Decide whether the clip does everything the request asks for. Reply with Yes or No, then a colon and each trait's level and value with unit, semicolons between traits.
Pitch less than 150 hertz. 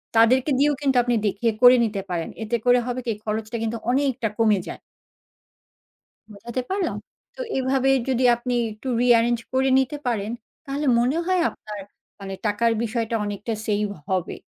No: high, 235 Hz